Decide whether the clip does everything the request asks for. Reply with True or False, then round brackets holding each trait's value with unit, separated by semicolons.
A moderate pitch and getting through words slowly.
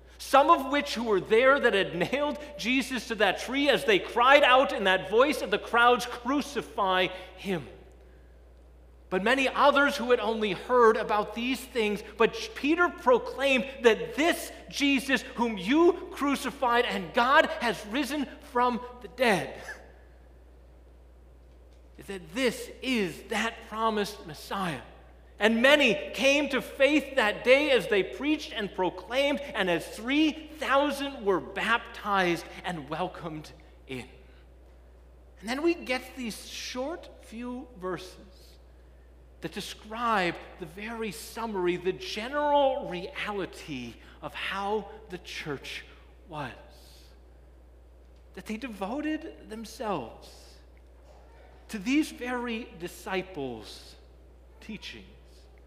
False (220 Hz; 115 wpm)